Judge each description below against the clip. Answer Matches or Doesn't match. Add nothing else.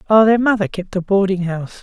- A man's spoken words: Doesn't match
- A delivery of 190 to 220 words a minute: Doesn't match